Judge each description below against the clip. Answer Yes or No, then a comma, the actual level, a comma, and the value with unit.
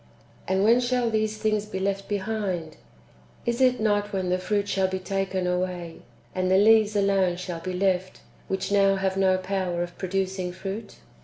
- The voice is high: Yes, high, 195 Hz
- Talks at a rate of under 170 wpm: No, average, 190 wpm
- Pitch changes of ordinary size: No, narrow, 2.0 semitones